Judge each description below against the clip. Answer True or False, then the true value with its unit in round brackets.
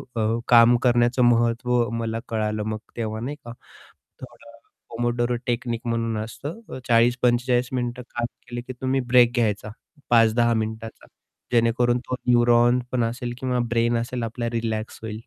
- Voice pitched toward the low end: True (120 Hz)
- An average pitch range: False (1.1 semitones)